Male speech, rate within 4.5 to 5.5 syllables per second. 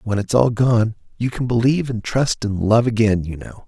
Yes: male; 5.1 syllables/s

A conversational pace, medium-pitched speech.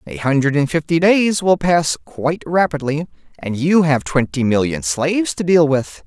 Yes: average, 180 wpm; medium, 155 Hz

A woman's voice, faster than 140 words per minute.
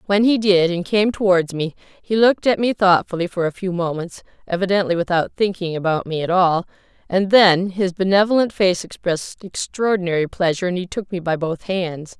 Yes: female; average, 185 wpm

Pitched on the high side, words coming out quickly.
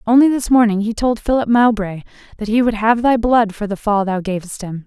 Yes: high, 220 Hz; fast, 235 wpm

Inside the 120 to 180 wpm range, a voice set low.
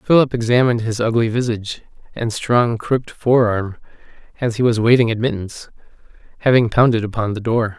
Yes: average, 155 wpm; low, 115 Hz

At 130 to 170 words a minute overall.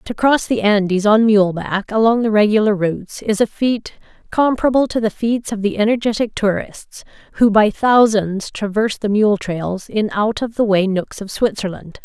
No: average, 185 wpm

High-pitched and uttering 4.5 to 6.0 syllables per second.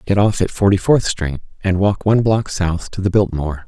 No: very low, 95 Hz; 5.4 syllables/s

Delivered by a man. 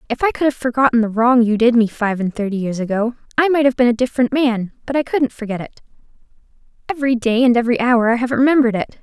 No: female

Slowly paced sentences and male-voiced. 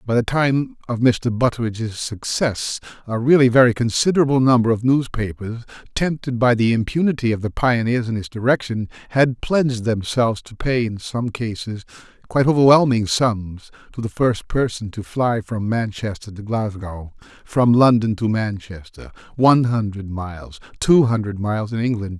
No: average, 160 wpm; male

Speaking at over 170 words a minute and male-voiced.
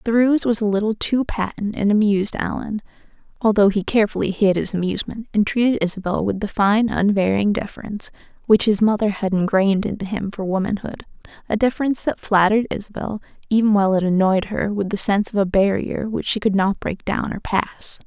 No: average, 185 wpm; female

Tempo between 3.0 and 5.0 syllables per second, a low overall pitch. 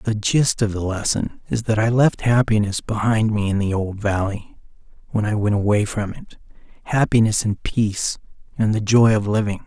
Yes: 4.9 syllables/s; low, 105 Hz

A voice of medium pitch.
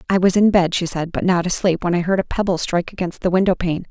Yes: medium, 180 Hz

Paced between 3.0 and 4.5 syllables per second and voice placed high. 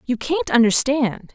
Yes: 4.1 syllables/s; very high, 255 Hz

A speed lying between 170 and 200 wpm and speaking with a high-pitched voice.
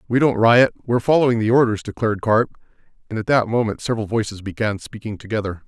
No: average, 190 wpm; low, 110 Hz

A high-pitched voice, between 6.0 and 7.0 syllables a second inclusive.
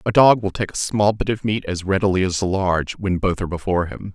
No: very low, 95 Hz; 6.2 syllables/s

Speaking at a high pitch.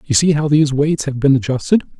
No: medium, 140 Hz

